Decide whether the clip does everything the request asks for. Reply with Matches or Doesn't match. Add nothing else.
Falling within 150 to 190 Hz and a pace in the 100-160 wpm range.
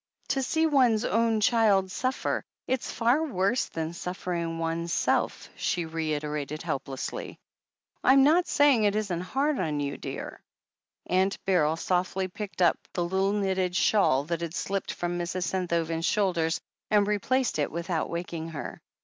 Matches